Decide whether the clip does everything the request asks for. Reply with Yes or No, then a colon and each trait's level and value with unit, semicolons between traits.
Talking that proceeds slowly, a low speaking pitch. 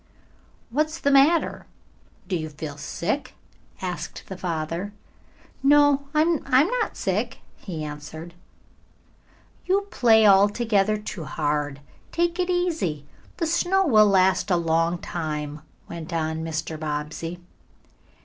No: slow, 115 wpm; medium, 185 Hz